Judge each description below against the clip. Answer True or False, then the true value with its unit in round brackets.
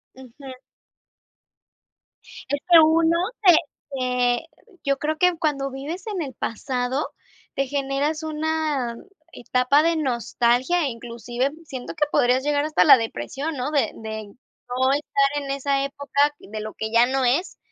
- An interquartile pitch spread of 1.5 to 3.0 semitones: False (3.5 semitones)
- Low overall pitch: False (275 Hz)